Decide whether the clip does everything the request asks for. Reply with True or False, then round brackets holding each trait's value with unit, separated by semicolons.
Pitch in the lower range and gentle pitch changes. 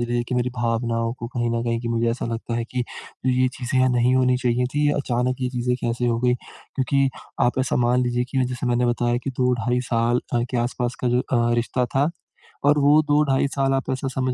True (125 Hz; 1.3 semitones)